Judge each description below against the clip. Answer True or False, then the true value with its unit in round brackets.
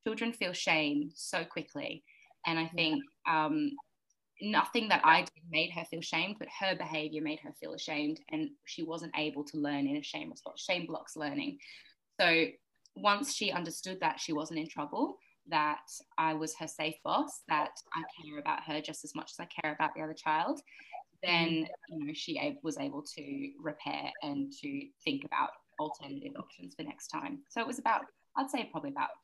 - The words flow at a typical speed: True (190 wpm)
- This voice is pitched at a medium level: True (165 Hz)